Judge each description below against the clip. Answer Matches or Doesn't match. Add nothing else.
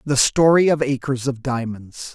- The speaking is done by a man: Matches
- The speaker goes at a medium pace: Matches